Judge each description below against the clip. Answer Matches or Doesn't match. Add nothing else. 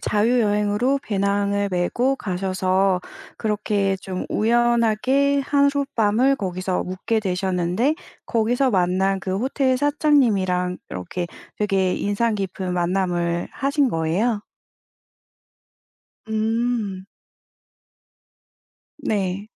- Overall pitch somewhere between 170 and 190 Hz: Doesn't match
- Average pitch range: Matches